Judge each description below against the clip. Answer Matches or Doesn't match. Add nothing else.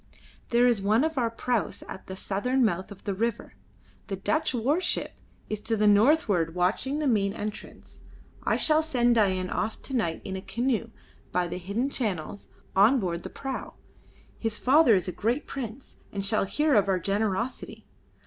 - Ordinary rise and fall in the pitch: Matches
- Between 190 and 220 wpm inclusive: Doesn't match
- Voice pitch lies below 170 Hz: Doesn't match